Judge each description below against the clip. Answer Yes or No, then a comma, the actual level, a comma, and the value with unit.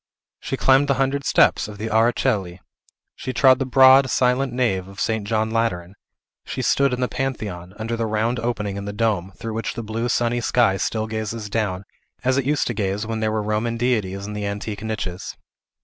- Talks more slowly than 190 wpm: No, fast, 205 wpm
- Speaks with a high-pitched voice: No, low, 110 Hz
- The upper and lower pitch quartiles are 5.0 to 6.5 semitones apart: No, average, 3.1 semitones